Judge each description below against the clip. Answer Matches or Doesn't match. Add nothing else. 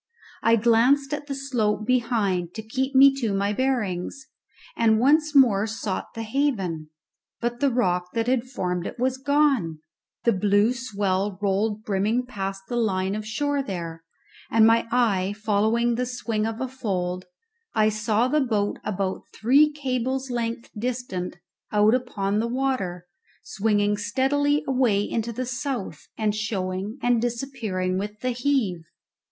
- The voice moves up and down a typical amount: Matches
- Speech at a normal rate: Matches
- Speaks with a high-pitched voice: Matches